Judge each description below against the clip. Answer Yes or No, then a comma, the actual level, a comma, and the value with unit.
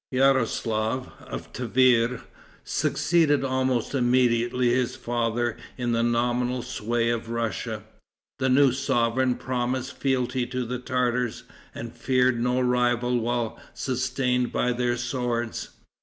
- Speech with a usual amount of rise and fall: No, narrow, 1.3 semitones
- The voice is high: No, low, 125 Hz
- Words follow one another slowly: Yes, slow, 115 wpm